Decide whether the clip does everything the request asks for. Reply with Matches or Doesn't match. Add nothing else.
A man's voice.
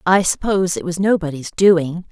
Doesn't match